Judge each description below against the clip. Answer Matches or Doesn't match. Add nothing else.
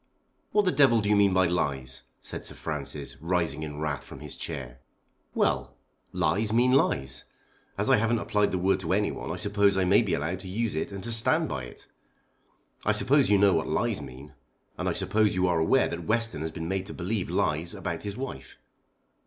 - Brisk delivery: Matches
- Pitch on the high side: Doesn't match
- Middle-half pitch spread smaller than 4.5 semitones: Doesn't match